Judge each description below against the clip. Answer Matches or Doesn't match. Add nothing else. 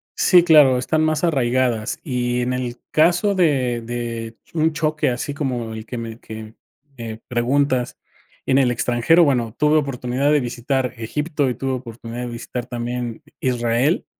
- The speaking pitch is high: Doesn't match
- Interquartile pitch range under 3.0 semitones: Doesn't match